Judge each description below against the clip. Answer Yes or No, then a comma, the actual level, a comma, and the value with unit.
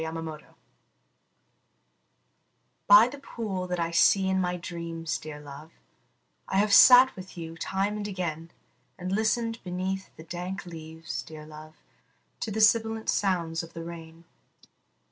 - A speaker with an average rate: Yes, average, 145 wpm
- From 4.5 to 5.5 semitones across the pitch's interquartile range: No, average, 3.6 semitones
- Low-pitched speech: No, medium, 180 Hz